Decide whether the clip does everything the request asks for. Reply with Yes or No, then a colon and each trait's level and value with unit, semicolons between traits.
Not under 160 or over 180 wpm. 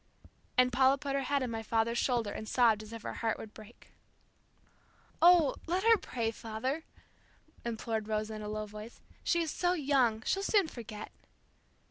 Yes: average, 175 wpm